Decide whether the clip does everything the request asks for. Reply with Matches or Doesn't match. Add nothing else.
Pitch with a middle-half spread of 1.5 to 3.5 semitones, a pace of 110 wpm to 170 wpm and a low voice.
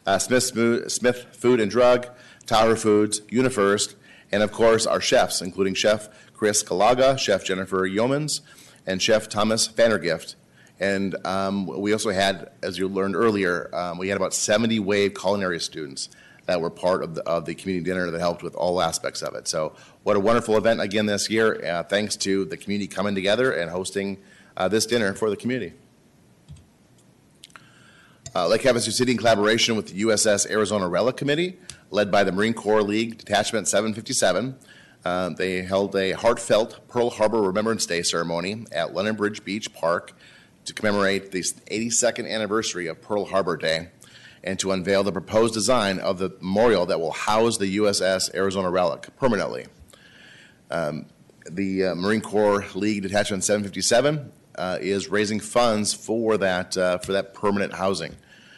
Matches